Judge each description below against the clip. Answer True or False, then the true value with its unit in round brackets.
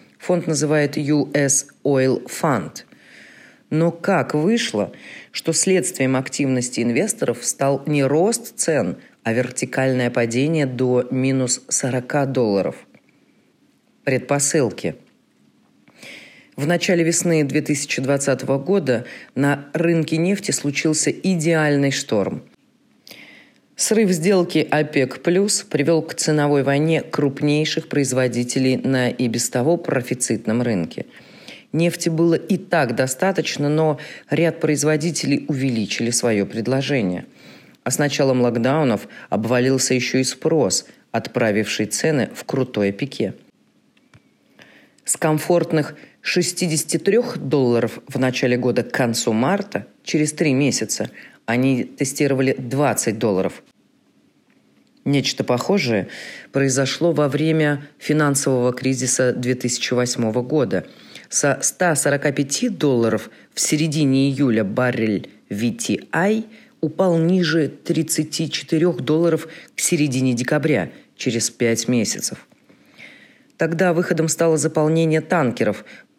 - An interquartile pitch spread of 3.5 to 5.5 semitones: True (3.9 semitones)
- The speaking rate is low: True (100 wpm)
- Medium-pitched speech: True (145 Hz)